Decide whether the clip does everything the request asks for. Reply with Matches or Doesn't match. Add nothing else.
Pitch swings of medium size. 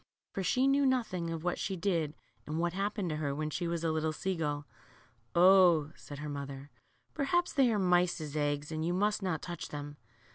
Matches